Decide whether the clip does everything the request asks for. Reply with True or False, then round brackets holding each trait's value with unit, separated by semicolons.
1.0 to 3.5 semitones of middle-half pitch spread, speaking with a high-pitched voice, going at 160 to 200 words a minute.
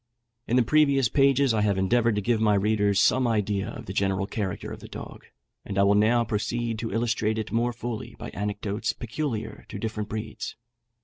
False (2.5 semitones; 110 Hz; 195 wpm)